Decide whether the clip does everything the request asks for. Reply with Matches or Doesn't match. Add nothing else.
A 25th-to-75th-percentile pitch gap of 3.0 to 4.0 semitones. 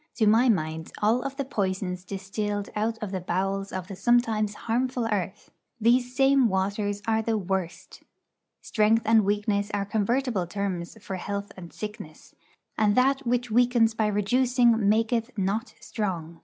Matches